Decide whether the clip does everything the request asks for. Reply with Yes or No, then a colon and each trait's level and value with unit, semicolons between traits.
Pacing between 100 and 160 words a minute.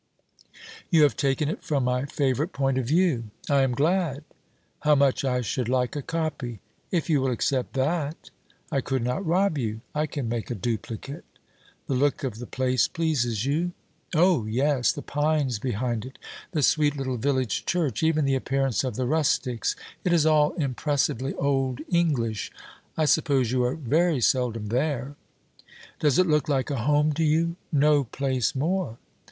No: average, 170 wpm